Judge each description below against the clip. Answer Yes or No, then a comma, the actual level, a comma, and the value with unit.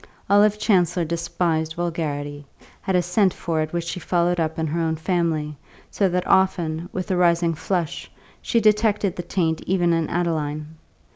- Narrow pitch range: Yes, narrow, 2.2 semitones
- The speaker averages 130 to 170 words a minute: Yes, average, 165 wpm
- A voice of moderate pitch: Yes, medium, 170 Hz